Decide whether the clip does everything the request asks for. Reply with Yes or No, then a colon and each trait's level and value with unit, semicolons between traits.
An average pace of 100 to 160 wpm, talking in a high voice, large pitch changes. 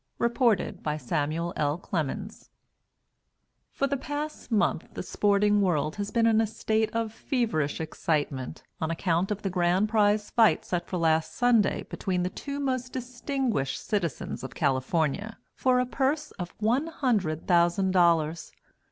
Yes: average, 150 wpm; high, 200 Hz; wide, 6.3 semitones